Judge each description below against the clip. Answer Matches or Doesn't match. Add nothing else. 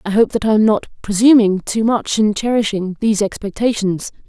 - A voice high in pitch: Matches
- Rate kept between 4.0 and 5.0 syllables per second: Doesn't match